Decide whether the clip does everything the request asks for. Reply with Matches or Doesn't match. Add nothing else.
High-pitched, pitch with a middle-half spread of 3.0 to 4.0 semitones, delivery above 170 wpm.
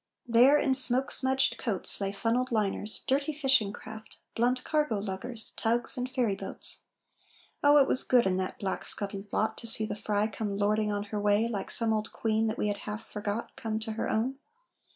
Matches